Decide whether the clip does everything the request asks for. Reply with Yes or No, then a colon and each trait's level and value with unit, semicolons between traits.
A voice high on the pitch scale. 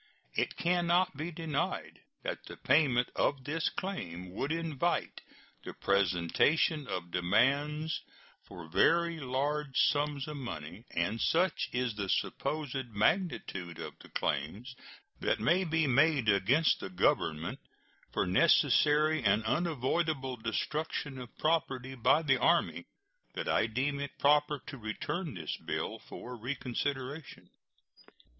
No: low, 135 Hz